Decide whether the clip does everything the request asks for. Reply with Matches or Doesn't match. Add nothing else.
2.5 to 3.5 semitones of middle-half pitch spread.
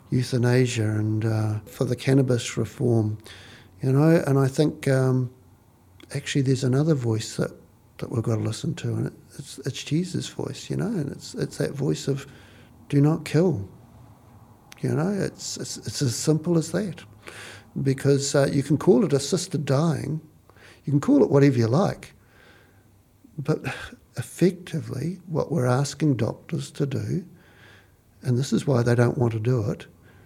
Doesn't match